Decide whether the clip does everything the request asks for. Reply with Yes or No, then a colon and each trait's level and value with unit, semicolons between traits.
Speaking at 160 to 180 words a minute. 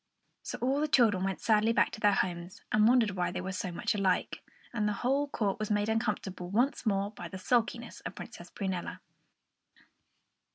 No: average, 190 wpm